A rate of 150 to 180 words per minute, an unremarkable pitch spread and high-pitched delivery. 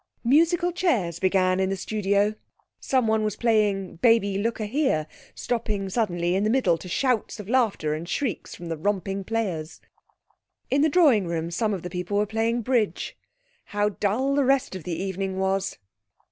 Yes: average, 175 wpm; average, 3.9 semitones; high, 205 Hz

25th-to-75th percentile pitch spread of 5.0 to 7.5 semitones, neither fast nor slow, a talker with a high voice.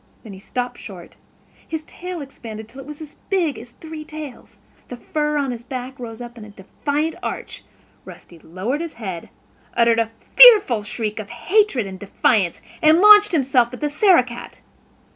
Yes: wide, 5.5 semitones; average, 180 wpm; very high, 250 Hz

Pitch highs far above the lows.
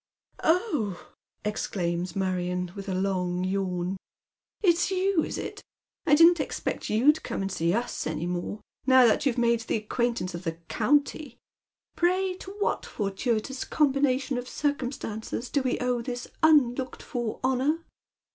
Yes: wide, 6.8 semitones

